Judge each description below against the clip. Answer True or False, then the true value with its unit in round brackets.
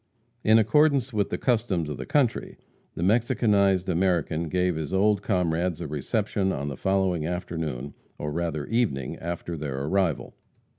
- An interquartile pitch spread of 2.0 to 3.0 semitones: False (4.8 semitones)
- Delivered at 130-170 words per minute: True (150 wpm)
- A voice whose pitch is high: False (90 Hz)